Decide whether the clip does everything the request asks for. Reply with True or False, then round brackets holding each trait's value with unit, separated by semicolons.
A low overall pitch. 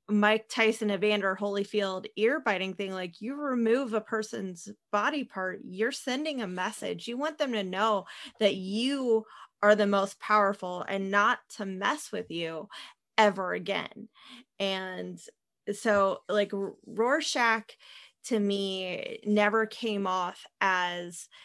False (210 Hz)